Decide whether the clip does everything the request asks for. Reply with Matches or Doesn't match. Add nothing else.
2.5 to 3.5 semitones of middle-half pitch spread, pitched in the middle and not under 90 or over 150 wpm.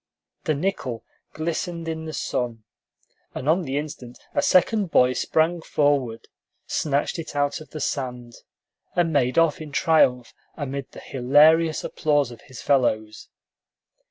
Doesn't match